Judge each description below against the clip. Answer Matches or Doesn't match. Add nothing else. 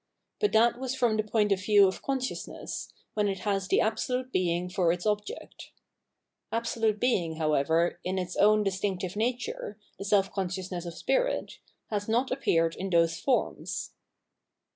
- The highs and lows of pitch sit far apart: Doesn't match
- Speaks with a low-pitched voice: Doesn't match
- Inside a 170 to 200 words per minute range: Doesn't match